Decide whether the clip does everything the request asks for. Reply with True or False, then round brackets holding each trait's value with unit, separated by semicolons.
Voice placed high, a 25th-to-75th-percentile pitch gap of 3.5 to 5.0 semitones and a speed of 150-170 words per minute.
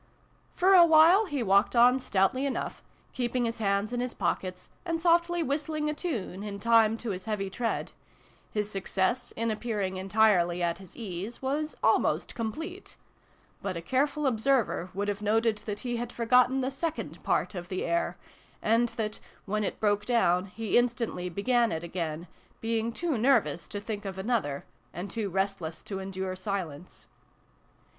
True (220 Hz; 4.7 semitones; 165 wpm)